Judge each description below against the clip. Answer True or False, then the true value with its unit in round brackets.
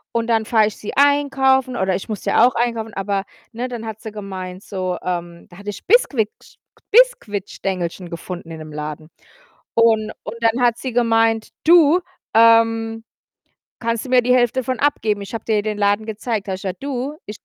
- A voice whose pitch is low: False (225 Hz)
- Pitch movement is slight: False (3.6 semitones)